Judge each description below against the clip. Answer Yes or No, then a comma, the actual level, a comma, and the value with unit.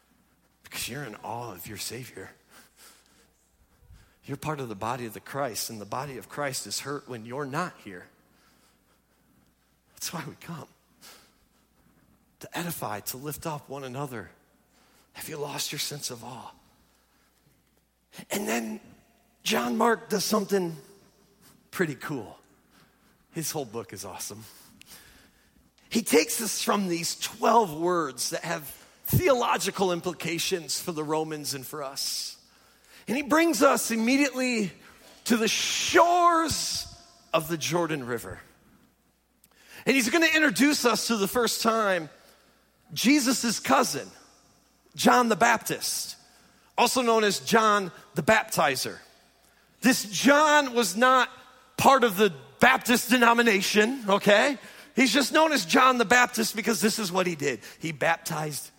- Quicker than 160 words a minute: No, slow, 135 wpm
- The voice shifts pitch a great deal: Yes, wide, 8.2 semitones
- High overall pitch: Yes, high, 200 Hz